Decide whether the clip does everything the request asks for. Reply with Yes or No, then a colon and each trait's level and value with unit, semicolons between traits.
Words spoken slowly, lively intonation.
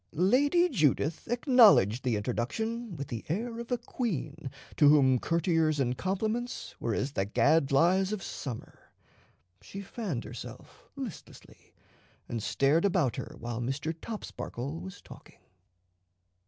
Yes: slow, 125 wpm; wide, 8.6 semitones